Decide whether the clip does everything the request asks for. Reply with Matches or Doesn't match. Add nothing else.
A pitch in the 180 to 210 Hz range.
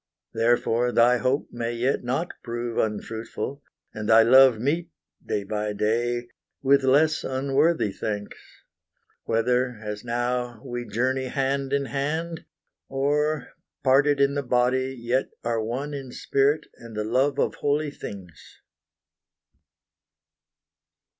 Doesn't match